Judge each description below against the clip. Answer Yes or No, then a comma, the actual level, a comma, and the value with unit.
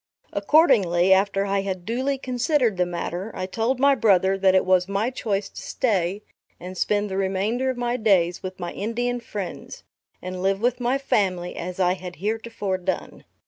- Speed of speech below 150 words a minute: No, average, 180 wpm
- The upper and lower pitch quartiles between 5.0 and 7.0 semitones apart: No, average, 4.1 semitones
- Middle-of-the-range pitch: No, high, 195 Hz